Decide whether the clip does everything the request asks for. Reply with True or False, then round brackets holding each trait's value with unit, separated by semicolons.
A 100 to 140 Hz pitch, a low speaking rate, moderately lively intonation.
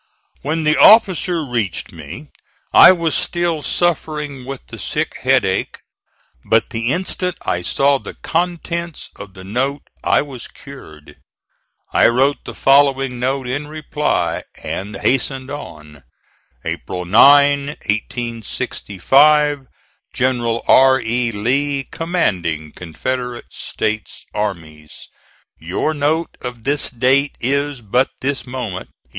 True (135 Hz; 115 wpm; 4.7 semitones)